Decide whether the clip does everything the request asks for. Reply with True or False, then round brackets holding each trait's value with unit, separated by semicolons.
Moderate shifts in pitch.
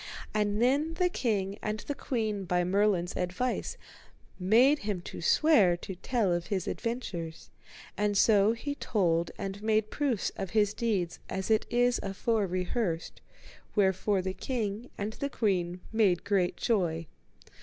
True (4.0 semitones)